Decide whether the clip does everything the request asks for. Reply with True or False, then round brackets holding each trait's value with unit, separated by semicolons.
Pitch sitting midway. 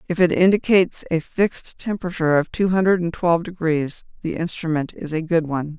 True (170 Hz)